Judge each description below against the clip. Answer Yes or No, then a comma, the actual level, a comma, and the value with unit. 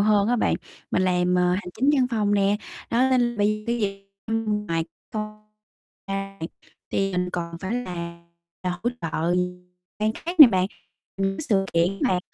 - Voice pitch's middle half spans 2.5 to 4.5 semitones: Yes, average, 3.4 semitones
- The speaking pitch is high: Yes, high, 205 Hz